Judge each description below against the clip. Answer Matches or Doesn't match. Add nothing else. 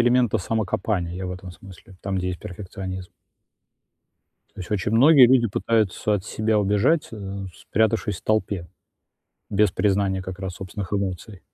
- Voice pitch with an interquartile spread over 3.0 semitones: Doesn't match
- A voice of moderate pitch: Doesn't match